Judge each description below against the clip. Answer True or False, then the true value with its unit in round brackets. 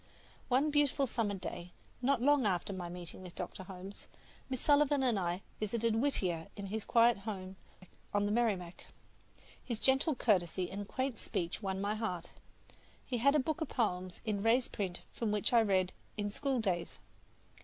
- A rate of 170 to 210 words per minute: True (175 wpm)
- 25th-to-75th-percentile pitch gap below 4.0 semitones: False (5.0 semitones)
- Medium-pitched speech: False (210 Hz)